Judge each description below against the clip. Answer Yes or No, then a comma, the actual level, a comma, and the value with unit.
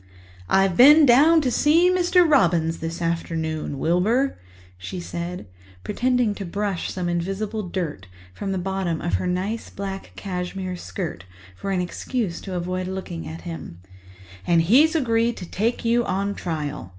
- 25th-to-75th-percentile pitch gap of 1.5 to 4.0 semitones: No, average, 5.3 semitones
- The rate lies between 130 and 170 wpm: Yes, average, 150 wpm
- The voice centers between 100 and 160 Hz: No, high, 190 Hz